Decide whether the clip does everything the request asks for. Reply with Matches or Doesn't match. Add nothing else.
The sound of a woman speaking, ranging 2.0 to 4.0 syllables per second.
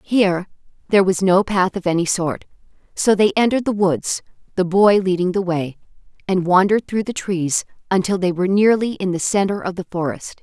Doesn't match